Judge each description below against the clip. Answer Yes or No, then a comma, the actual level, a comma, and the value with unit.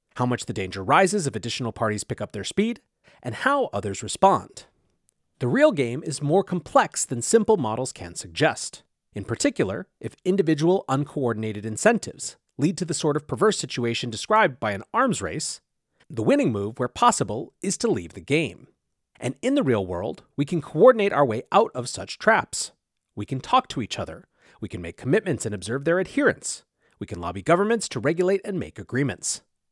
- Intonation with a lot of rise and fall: Yes, wide, 8.4 semitones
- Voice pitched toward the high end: No, medium, 140 Hz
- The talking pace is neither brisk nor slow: Yes, average, 185 wpm